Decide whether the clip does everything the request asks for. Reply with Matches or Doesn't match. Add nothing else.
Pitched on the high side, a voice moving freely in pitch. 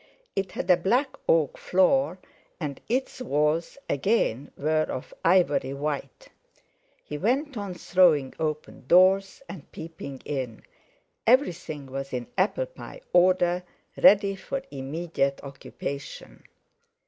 Doesn't match